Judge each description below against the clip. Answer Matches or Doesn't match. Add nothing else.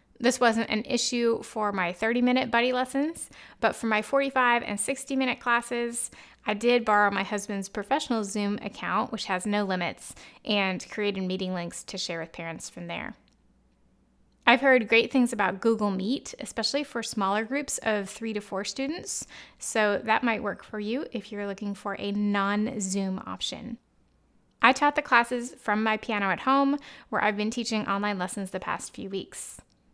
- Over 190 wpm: Doesn't match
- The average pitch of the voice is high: Matches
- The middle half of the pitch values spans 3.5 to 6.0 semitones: Doesn't match